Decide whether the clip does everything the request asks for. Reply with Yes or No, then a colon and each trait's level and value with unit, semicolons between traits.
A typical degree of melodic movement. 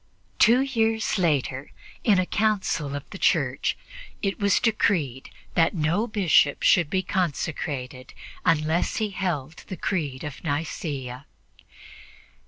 No: wide, 5.8 semitones